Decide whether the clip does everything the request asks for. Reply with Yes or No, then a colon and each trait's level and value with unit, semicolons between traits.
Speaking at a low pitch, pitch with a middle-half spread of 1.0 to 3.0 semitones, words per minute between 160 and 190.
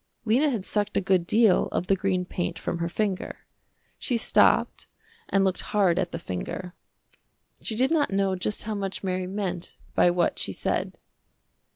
No: high, 190 Hz; average, 2.7 semitones; average, 175 wpm